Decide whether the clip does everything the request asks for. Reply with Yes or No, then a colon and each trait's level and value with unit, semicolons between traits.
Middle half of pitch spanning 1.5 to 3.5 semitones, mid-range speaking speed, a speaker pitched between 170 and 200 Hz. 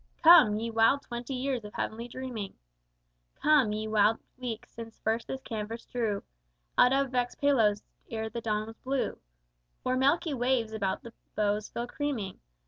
No: average, 3.2 semitones; average, 165 wpm; high, 230 Hz